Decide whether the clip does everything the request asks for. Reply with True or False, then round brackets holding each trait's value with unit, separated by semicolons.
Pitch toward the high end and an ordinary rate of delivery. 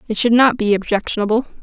True (225 Hz; 185 wpm)